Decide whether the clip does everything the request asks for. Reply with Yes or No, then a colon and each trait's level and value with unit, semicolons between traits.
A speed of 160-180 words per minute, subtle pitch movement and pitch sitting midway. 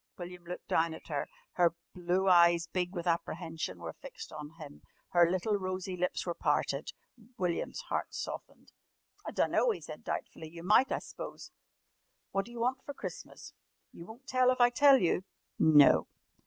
No: average, 170 wpm; average, 3.9 semitones; medium, 180 Hz